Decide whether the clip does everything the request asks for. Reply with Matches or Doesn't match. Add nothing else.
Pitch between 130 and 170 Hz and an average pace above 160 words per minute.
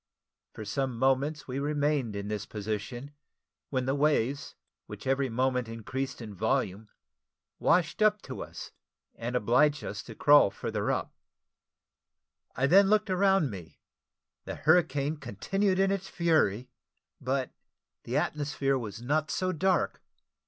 Doesn't match